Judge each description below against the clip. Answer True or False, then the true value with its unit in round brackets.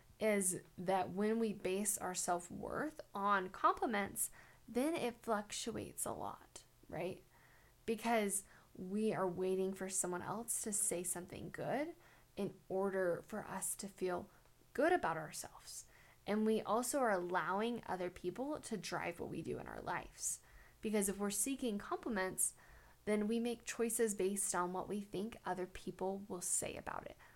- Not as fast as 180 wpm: True (155 wpm)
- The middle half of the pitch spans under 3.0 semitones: False (3.5 semitones)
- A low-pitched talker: False (200 Hz)